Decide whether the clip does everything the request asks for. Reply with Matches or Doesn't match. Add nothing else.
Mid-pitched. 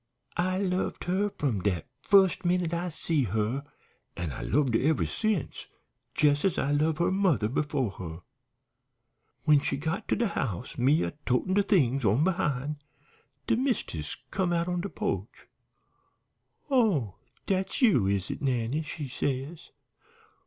Matches